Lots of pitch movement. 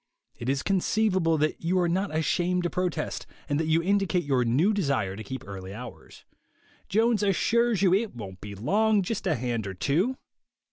Yes: wide, 7.8 semitones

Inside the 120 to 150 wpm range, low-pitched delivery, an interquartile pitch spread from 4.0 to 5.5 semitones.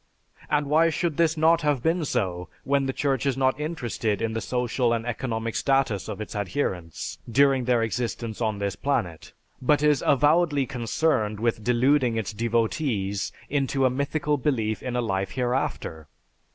No: average, 165 wpm; low, 125 Hz; average, 4.5 semitones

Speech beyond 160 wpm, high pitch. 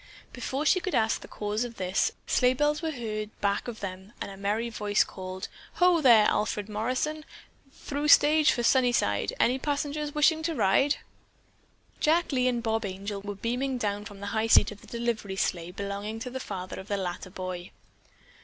Yes: average, 185 wpm; high, 225 Hz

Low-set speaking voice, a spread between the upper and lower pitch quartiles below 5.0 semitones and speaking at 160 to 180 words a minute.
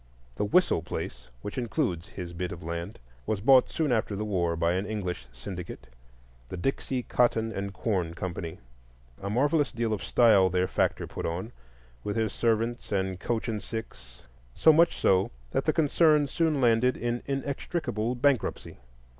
No: low, 110 Hz; average, 5.3 semitones; average, 165 wpm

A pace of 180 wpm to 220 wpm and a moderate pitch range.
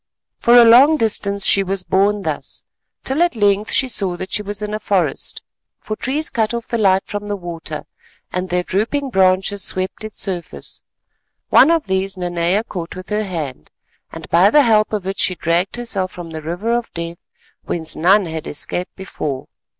Yes: average, 190 wpm; average, 3.4 semitones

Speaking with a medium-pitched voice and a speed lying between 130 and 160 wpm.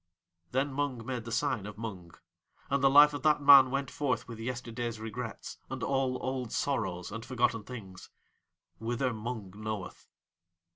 No: low, 120 Hz; average, 155 wpm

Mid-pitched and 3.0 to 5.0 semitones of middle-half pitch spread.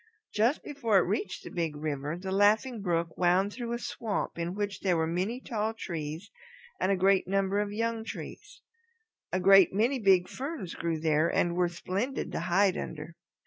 No: high, 195 Hz; average, 4.0 semitones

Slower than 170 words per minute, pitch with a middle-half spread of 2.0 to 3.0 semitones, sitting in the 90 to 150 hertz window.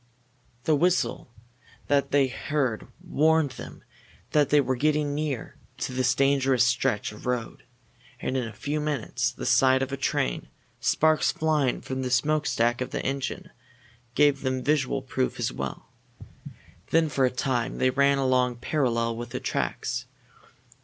Yes: average, 155 wpm; average, 2.7 semitones; low, 135 Hz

